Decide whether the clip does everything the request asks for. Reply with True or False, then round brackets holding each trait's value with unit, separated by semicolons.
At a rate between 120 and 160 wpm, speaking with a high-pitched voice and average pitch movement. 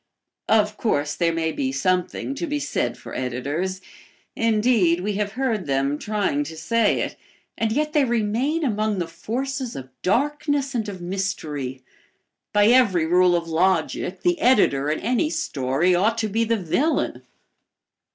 False (155 wpm; 205 Hz; 6.6 semitones)